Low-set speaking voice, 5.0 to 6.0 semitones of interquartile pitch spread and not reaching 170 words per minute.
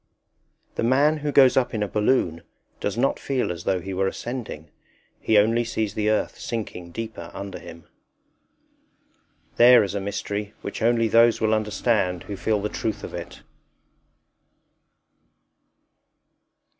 No: low, 110 Hz; average, 3.0 semitones; average, 145 wpm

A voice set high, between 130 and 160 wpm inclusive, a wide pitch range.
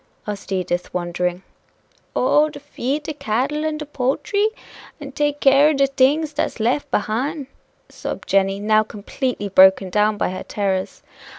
Yes: very high, 250 Hz; average, 155 wpm; wide, 6.8 semitones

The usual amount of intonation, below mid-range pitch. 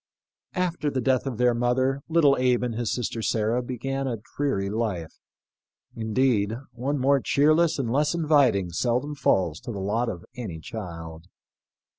Yes: average, 4.3 semitones; low, 125 Hz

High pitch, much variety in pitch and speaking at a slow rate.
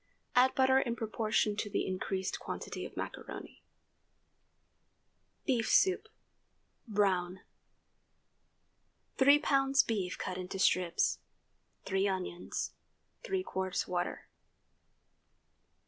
Yes: high, 210 Hz; wide, 6.0 semitones; slow, 90 wpm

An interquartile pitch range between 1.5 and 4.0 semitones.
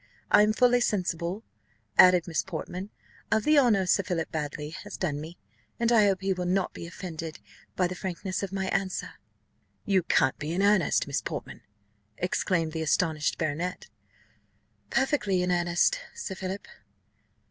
Yes: average, 2.9 semitones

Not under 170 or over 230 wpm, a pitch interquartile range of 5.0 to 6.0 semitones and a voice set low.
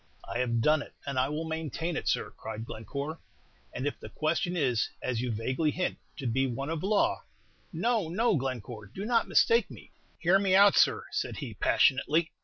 No: average, 200 wpm; wide, 5.5 semitones; medium, 150 Hz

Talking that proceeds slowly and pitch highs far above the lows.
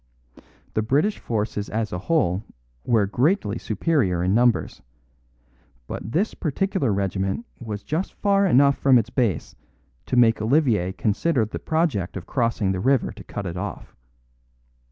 No: average, 145 wpm; wide, 6.0 semitones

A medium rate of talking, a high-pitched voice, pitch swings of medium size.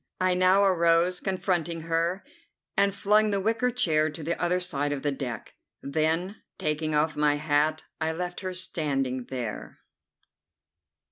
No: average, 145 wpm; medium, 165 Hz; average, 3.5 semitones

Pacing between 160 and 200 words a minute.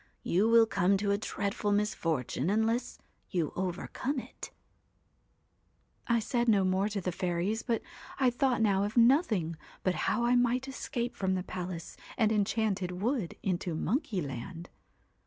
No: average, 145 wpm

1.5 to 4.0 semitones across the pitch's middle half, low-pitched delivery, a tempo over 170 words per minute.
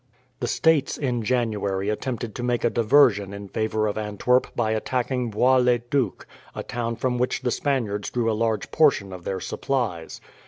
Yes: average, 3.1 semitones; low, 115 Hz; average, 180 wpm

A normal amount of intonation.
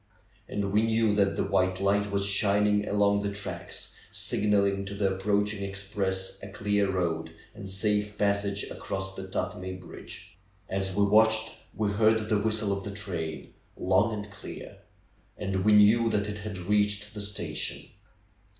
No: narrow, 1.4 semitones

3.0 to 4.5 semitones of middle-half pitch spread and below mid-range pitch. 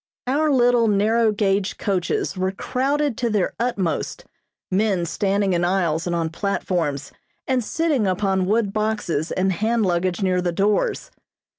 No: average, 3.8 semitones; high, 200 Hz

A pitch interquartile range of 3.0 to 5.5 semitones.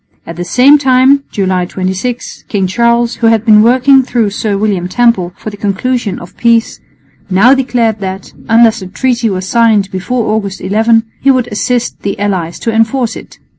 Yes: average, 3.8 semitones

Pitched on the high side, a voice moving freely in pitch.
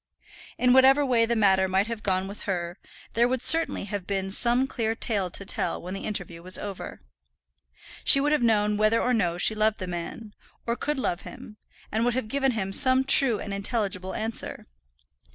No: high, 215 Hz; average, 4.1 semitones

